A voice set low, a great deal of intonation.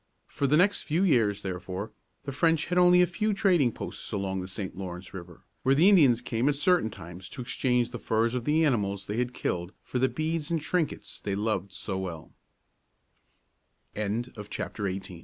Yes: low, 120 Hz; wide, 8.3 semitones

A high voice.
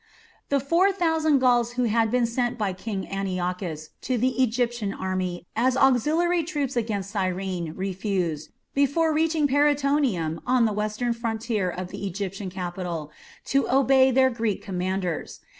Yes: high, 230 Hz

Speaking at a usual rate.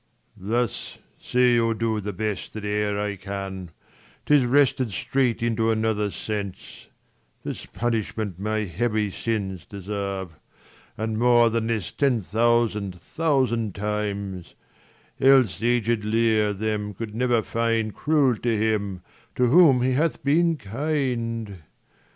No: slow, 130 wpm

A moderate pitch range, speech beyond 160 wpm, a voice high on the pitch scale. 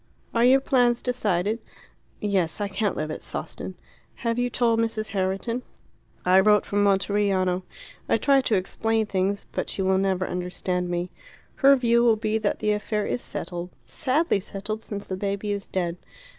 Yes: average, 3.4 semitones; average, 170 wpm; high, 205 Hz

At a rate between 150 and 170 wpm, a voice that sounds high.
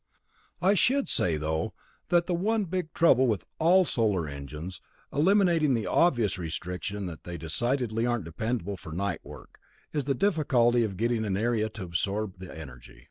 No: average, 165 wpm; low, 110 Hz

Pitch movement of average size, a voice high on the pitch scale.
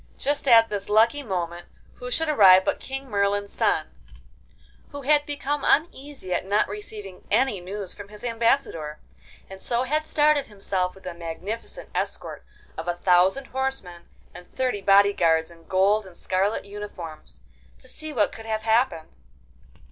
No: wide, 5.9 semitones; high, 205 Hz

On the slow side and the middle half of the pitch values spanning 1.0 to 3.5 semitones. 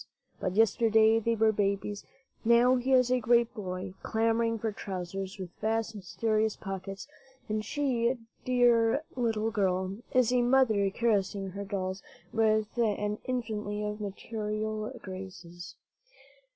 Yes: slow, 125 wpm; average, 2.8 semitones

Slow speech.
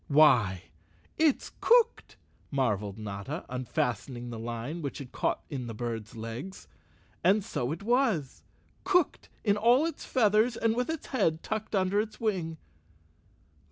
Yes: slow, 130 wpm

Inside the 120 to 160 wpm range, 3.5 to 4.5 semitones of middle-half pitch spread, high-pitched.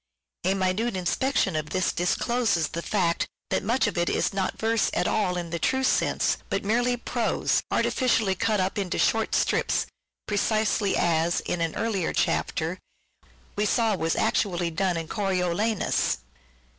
Yes: average, 155 wpm; average, 4.1 semitones; high, 195 Hz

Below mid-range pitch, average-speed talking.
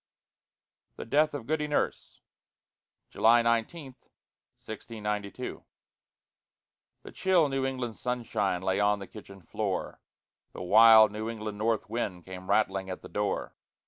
No: low, 110 Hz; slow, 125 wpm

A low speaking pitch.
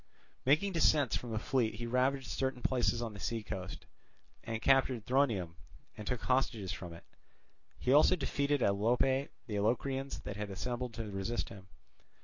Yes: low, 120 Hz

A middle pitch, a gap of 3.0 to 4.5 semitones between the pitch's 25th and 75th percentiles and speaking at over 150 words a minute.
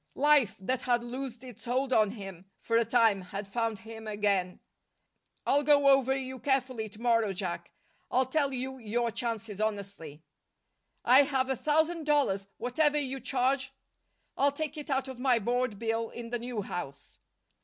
No: high, 240 Hz; average, 3.8 semitones; average, 170 wpm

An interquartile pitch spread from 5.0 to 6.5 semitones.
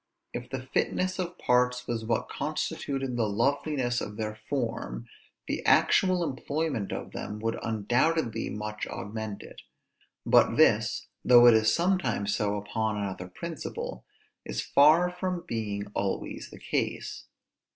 Yes: average, 5.3 semitones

